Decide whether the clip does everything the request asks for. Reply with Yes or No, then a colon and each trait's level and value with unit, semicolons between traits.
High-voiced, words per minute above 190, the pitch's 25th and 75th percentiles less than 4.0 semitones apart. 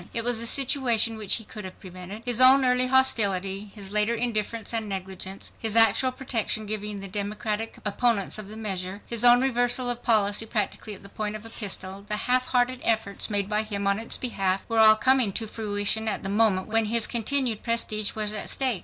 Yes: high, 220 Hz; fast, 205 wpm; average, 2.7 semitones